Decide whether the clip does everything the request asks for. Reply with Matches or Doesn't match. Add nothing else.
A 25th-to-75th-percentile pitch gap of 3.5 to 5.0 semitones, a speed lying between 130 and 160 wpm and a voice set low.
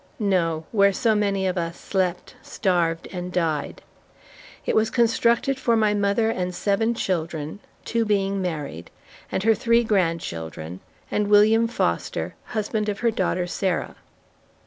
Doesn't match